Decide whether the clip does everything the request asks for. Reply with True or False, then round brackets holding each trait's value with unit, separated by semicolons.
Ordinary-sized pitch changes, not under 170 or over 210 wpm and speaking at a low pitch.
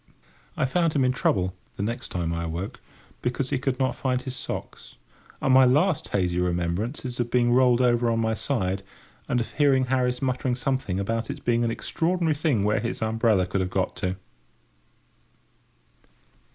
True (4.8 semitones; 180 wpm; 120 Hz)